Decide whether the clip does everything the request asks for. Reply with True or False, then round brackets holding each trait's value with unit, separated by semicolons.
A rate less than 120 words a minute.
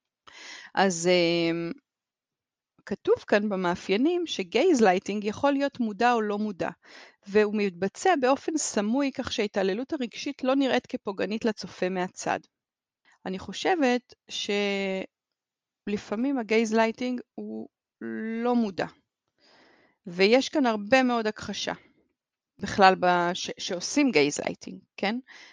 True (100 wpm)